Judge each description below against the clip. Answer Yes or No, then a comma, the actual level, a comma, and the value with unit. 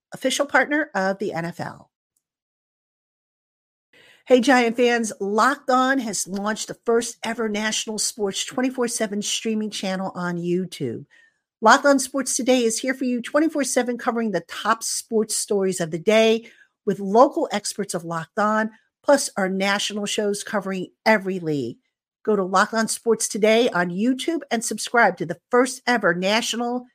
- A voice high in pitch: Yes, high, 220 Hz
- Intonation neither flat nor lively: Yes, average, 4.0 semitones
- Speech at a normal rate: Yes, average, 150 wpm